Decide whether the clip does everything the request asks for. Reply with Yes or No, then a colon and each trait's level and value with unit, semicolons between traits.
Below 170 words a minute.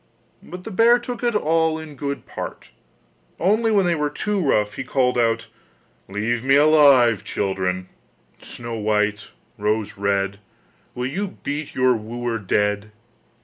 Yes: average, 145 wpm